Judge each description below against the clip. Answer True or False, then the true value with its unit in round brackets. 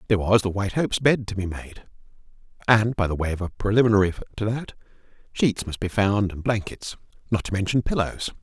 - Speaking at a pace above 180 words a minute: True (200 wpm)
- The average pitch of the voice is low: True (105 Hz)